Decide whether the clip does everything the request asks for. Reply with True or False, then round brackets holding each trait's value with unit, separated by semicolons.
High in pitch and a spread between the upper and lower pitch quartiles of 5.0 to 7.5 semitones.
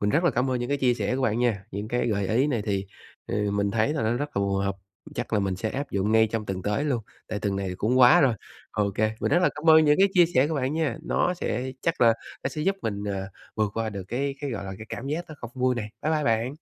False (115 Hz; 5.4 semitones)